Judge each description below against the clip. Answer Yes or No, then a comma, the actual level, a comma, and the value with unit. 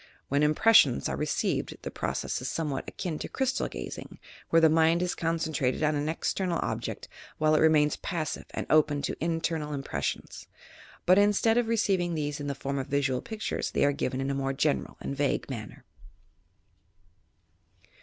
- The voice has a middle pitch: Yes, medium, 155 Hz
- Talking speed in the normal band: Yes, average, 175 wpm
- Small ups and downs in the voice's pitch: No, average, 3.2 semitones